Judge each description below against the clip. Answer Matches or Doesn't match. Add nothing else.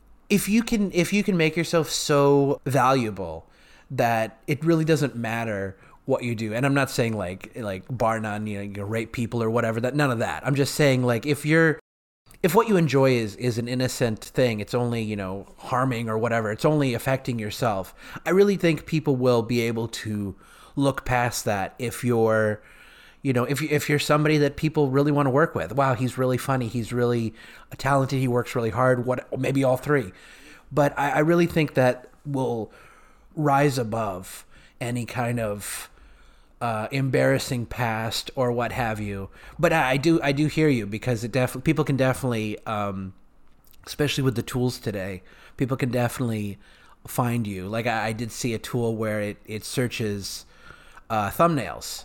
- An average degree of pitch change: Matches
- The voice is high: Doesn't match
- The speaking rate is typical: Matches